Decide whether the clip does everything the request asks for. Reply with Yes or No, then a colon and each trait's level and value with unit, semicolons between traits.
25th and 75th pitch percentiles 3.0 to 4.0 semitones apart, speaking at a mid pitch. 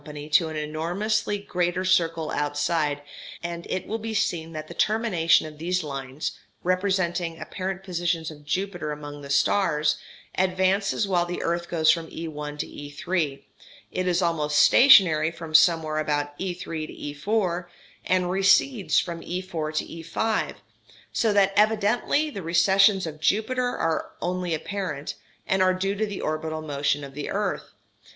Yes: average, 3.7 semitones; medium, 170 Hz